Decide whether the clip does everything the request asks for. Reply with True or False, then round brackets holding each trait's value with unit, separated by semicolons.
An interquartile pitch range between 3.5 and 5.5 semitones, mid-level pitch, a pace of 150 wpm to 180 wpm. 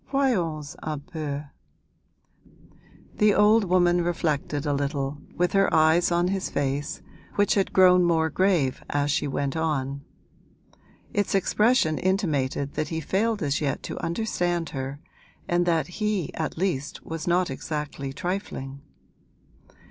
False (4.4 semitones; 160 Hz; 135 wpm)